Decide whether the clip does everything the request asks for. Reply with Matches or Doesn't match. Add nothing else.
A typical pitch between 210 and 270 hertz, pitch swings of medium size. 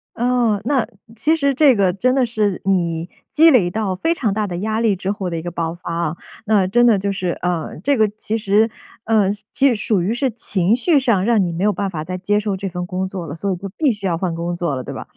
Doesn't match